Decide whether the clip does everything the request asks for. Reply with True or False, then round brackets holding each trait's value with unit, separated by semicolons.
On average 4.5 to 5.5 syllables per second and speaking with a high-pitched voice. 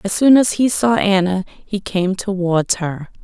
False (4.0 syllables/s; 195 Hz)